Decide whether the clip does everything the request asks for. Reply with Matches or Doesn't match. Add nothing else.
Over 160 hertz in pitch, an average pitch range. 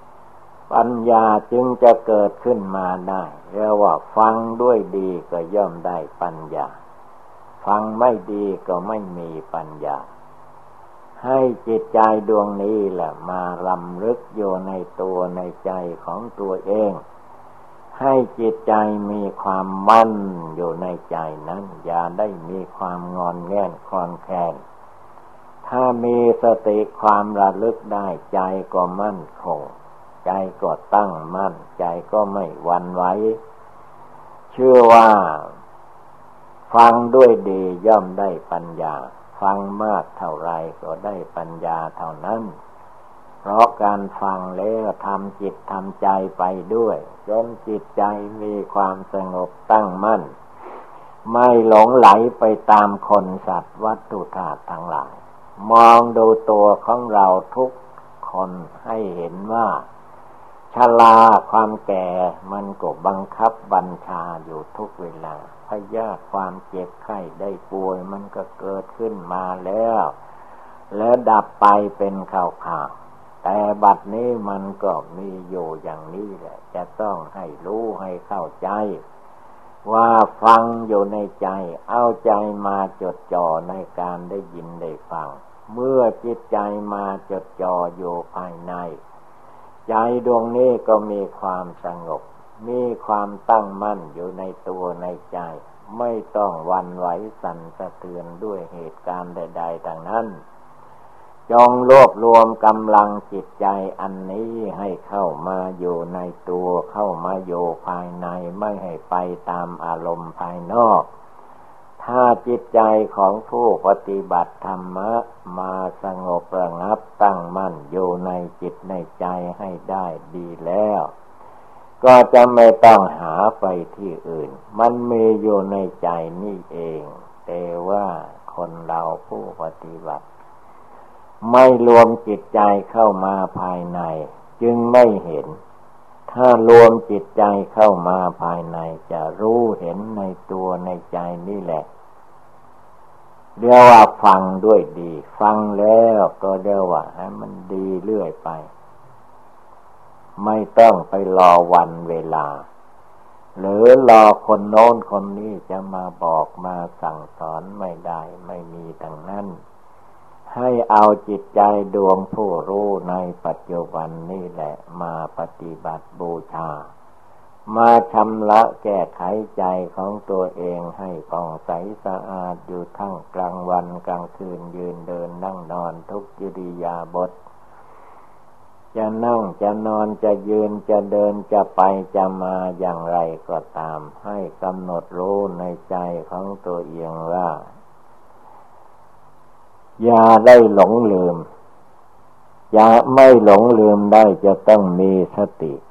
Doesn't match